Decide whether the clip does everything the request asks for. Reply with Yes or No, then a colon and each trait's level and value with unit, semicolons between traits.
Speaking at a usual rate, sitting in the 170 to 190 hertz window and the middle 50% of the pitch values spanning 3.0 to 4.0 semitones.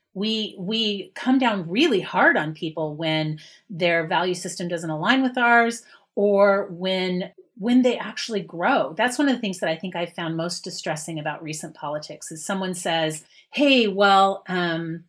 No: average, 170 wpm; medium, 185 Hz; average, 4.8 semitones